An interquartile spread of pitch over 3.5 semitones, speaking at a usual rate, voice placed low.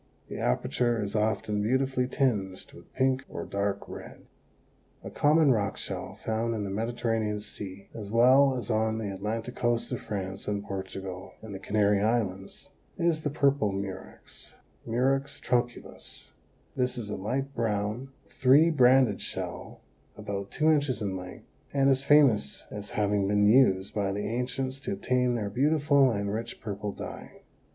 Yes: average, 4.4 semitones; average, 155 wpm; low, 110 Hz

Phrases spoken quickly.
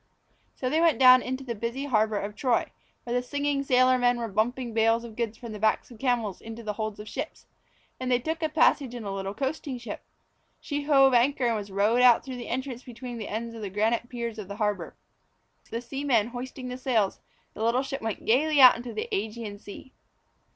Yes: fast, 220 wpm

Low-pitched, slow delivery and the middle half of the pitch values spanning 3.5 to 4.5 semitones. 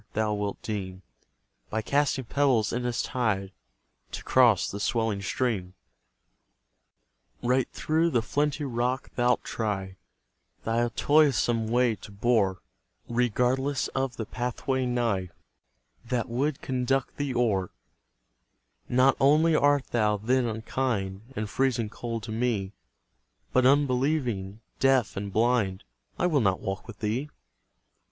Yes: low, 120 Hz; slow, 125 wpm; average, 3.8 semitones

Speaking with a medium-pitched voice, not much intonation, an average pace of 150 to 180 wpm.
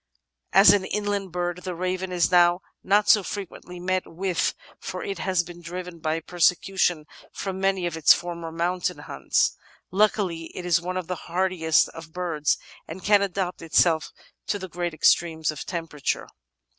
Yes: medium, 180 Hz; narrow, 2.1 semitones; average, 160 wpm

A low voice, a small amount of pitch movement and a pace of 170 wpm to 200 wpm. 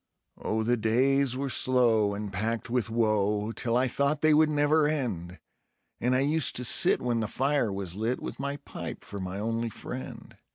No: low, 120 Hz; average, 4.2 semitones; average, 190 wpm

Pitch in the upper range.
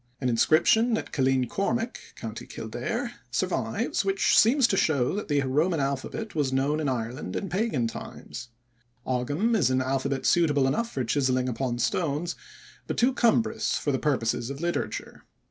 No: medium, 145 Hz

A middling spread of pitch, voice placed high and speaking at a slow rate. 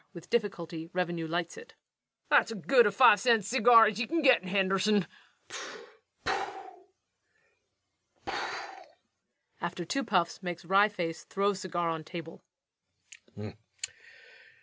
No: wide, 5.9 semitones; high, 200 Hz; slow, 120 wpm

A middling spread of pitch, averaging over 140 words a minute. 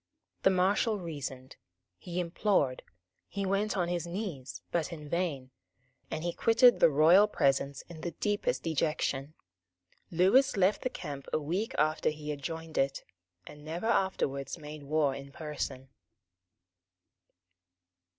No: average, 4.7 semitones; slow, 135 wpm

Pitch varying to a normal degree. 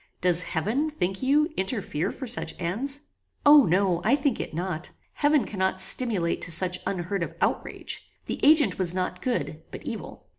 No: wide, 7.2 semitones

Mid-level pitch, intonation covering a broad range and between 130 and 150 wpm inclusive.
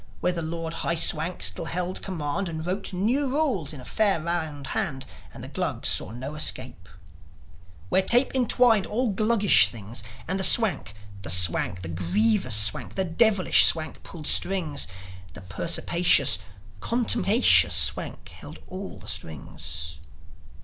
Yes: medium, 170 Hz; wide, 7.5 semitones; average, 145 wpm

